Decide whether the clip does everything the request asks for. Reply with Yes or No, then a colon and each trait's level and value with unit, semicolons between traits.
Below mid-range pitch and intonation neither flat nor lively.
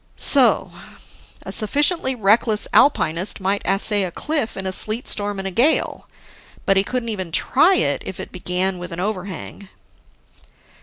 No: high, 205 Hz; average, 4.2 semitones